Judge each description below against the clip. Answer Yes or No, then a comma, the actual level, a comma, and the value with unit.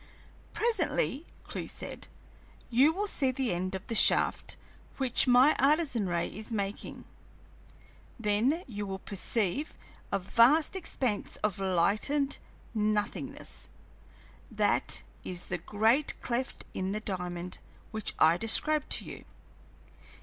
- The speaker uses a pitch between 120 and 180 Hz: No, high, 220 Hz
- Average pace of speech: No, slow, 120 wpm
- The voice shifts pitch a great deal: Yes, wide, 6.0 semitones